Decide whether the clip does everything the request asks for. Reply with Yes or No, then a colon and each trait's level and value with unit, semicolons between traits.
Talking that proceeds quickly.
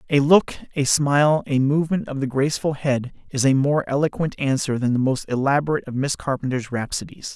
No: average, 190 wpm